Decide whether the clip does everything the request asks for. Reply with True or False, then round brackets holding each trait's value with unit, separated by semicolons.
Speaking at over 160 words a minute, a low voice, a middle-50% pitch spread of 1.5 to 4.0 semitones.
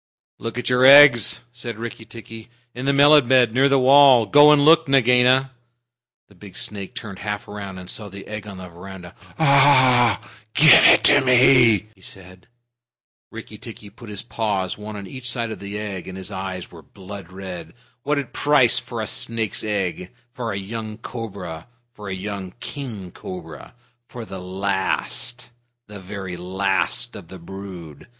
False (170 wpm; 105 Hz; 4.6 semitones)